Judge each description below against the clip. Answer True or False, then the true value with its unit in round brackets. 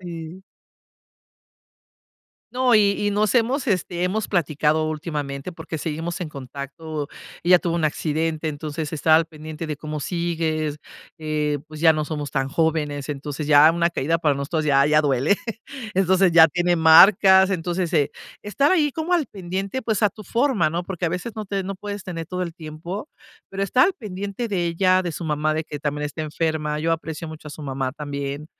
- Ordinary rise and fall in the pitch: True (3.7 semitones)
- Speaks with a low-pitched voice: False (165 Hz)